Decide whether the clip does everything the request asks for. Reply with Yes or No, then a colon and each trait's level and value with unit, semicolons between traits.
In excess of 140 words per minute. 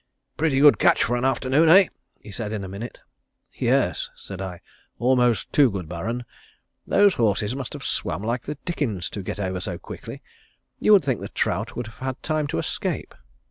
Yes: average, 190 wpm